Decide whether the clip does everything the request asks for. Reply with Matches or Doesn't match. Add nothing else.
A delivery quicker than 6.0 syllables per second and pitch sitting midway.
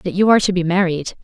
Matches